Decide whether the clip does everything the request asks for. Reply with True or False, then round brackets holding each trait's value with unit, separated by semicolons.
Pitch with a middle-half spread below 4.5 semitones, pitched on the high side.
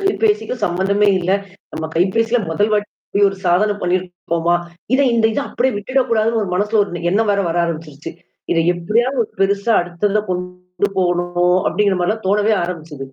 True (3.5 semitones; 195 Hz)